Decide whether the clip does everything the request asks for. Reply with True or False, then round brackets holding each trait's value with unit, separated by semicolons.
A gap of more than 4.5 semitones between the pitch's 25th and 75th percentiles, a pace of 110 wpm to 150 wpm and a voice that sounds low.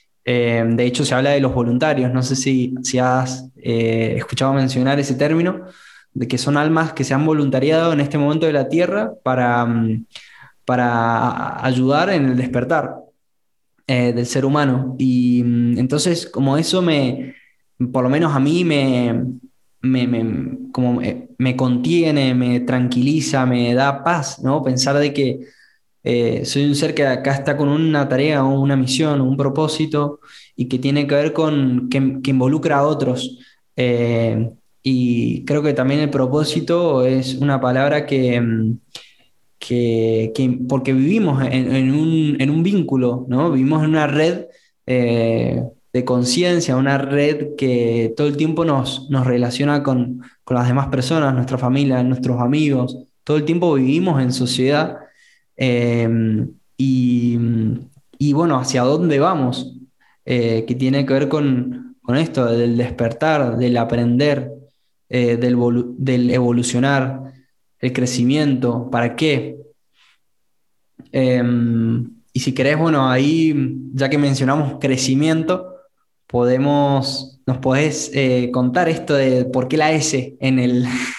False (2.7 semitones; 145 wpm; 130 Hz)